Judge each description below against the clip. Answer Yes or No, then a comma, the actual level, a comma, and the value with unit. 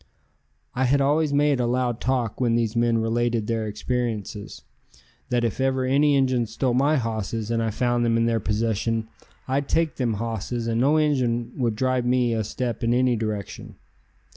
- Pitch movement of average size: No, narrow, 2.3 semitones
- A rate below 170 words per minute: No, average, 180 wpm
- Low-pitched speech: Yes, low, 120 Hz